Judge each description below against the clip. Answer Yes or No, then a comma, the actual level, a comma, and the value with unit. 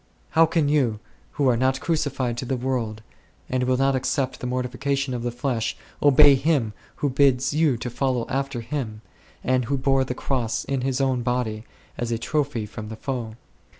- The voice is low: Yes, low, 130 Hz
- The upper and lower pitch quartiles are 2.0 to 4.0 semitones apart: Yes, narrow, 2.4 semitones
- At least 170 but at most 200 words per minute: Yes, average, 185 wpm